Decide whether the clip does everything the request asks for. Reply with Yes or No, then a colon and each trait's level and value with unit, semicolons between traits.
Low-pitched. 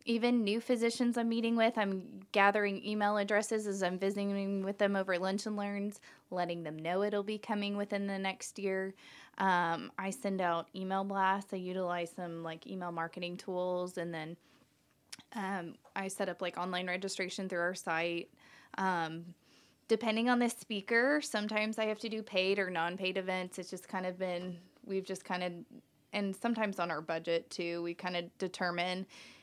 No: high, 190 Hz